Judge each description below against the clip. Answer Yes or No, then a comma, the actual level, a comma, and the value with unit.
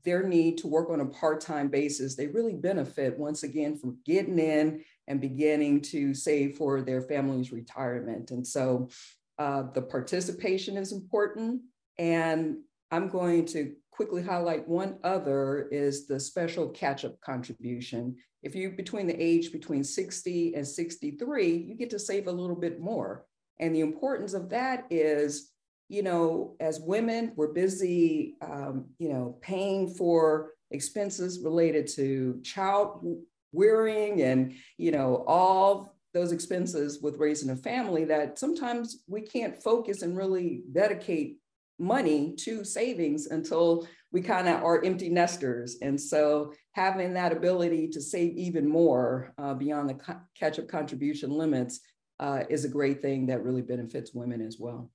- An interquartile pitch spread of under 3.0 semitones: No, average, 5.0 semitones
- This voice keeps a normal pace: Yes, average, 150 wpm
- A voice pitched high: No, medium, 160 Hz